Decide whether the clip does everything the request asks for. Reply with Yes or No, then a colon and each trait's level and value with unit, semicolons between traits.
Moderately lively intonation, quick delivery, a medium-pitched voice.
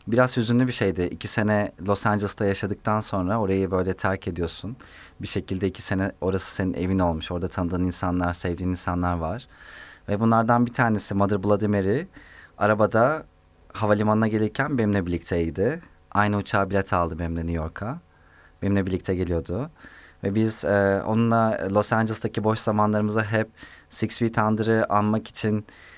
No: average, 3.3 semitones; fast, 145 wpm; low, 100 Hz